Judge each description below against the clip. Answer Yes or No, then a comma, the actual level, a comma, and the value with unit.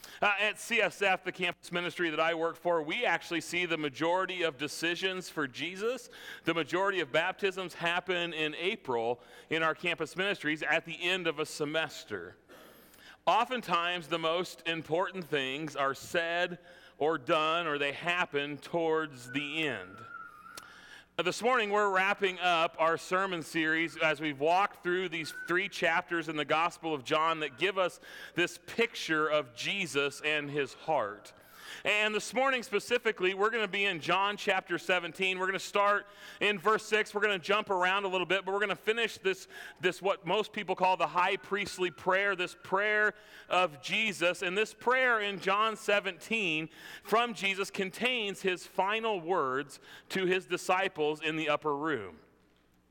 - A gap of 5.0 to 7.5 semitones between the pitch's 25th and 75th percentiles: No, average, 3.9 semitones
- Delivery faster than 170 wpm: No, average, 165 wpm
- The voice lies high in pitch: No, medium, 180 Hz